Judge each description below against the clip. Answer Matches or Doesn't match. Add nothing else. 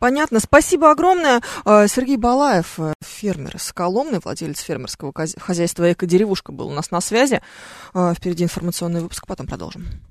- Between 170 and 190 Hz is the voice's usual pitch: Matches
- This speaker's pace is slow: Doesn't match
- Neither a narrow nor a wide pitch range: Doesn't match